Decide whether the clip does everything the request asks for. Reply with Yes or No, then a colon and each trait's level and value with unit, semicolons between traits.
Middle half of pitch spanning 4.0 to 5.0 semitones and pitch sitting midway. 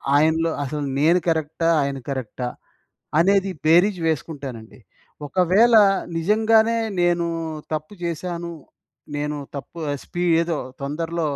No: average, 3.3 semitones; medium, 165 Hz